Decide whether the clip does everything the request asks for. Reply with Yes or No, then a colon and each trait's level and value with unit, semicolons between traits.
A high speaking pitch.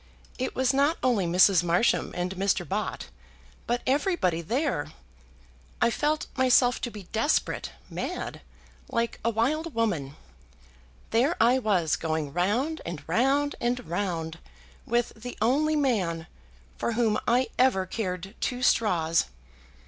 Yes: high, 230 Hz